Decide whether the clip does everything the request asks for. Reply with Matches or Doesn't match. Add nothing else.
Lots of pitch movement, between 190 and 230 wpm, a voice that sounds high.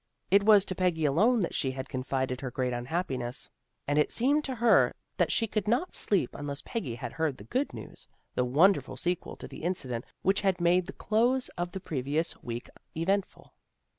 Doesn't match